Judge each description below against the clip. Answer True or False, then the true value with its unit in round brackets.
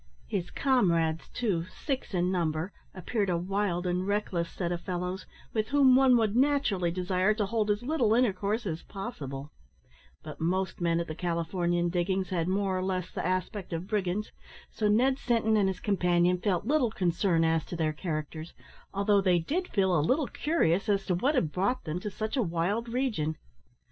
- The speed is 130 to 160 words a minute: False (185 wpm)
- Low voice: False (190 Hz)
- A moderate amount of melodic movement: True (3.9 semitones)